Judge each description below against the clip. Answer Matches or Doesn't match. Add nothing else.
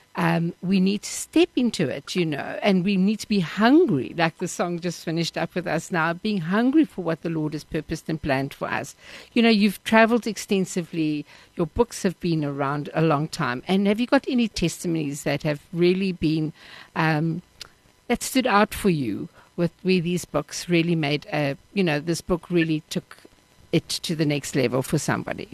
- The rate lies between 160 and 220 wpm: Matches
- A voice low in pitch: Doesn't match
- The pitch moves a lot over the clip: Doesn't match